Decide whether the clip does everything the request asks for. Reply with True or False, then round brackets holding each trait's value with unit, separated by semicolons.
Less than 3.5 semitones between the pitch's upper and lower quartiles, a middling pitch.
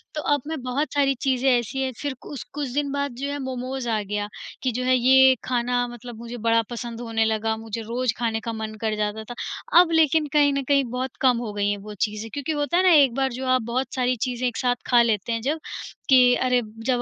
False (2.8 semitones; 250 Hz)